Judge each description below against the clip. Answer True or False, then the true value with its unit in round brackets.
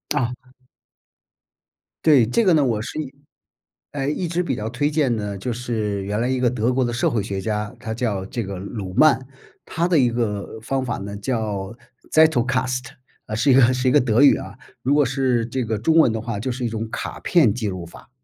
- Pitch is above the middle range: False (120 Hz)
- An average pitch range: True (3.6 semitones)